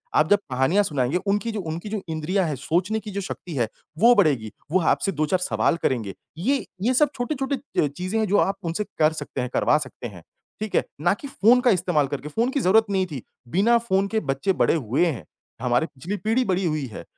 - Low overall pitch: No, medium, 185 Hz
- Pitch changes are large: Yes, wide, 6.5 semitones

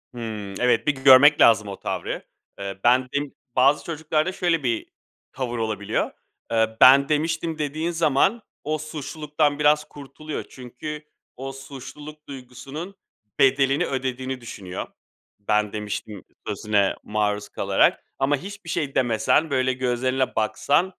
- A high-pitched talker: No, low, 135 Hz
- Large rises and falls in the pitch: No, average, 4.2 semitones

